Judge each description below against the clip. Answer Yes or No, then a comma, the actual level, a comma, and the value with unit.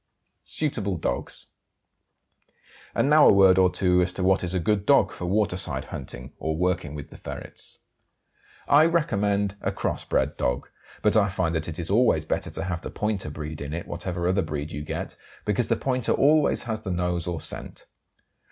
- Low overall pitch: Yes, very low, 95 Hz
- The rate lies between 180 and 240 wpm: Yes, average, 190 wpm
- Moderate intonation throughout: Yes, average, 4.0 semitones